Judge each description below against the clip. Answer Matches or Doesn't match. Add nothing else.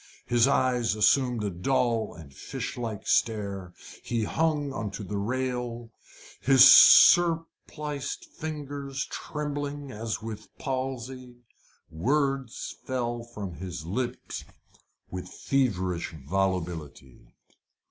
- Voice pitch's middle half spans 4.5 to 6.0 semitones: Matches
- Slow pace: Matches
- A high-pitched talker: Doesn't match